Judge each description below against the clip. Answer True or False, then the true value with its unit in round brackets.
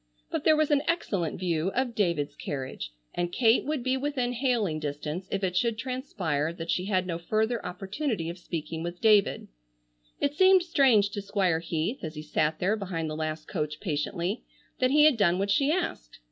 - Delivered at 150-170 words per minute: False (190 wpm)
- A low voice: False (195 Hz)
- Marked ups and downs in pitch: True (7.1 semitones)